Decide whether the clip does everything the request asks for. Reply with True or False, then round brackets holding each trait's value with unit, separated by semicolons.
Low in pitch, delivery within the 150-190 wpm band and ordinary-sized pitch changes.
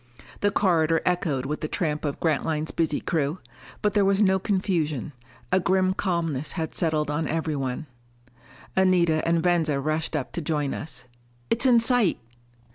False (165 Hz; 155 wpm; 3.7 semitones)